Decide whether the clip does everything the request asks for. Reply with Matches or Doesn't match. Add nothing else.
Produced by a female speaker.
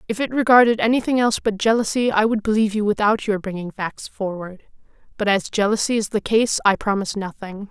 Matches